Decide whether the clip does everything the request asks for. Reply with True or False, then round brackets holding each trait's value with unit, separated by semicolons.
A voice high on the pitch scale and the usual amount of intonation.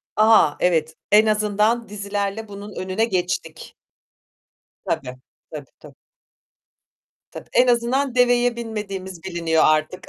True (205 Hz; 4.2 semitones)